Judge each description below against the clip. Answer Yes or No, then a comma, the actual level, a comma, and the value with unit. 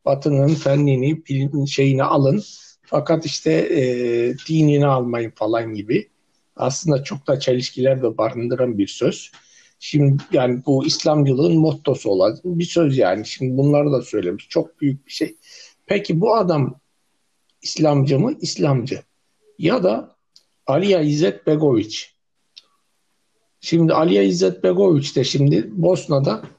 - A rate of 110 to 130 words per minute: Yes, average, 120 wpm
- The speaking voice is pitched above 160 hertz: No, medium, 140 Hz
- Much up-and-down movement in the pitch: No, average, 3.5 semitones